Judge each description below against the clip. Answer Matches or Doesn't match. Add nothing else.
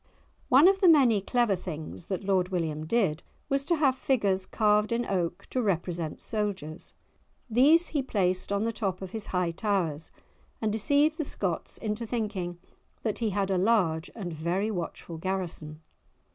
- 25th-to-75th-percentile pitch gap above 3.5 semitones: Matches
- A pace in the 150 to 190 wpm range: Matches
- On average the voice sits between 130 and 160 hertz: Doesn't match